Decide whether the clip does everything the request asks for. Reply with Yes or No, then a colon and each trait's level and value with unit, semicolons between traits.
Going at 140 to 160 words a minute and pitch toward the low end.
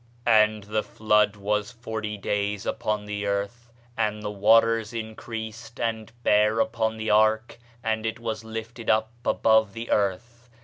Yes: average, 145 wpm; low, 110 Hz